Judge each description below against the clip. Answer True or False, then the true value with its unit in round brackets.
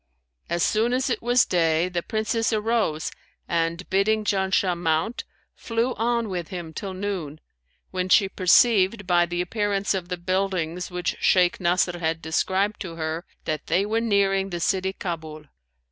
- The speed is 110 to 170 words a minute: True (160 wpm)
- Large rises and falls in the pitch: False (3.3 semitones)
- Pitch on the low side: False (185 Hz)